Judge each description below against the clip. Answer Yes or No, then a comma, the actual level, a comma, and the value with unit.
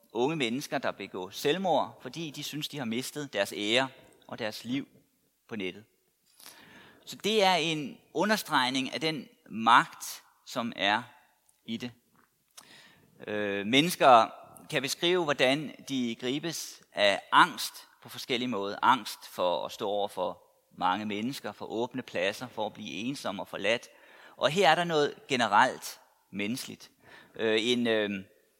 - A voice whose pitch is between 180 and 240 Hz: No, low, 135 Hz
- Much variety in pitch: Yes, wide, 6.8 semitones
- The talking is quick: No, slow, 145 wpm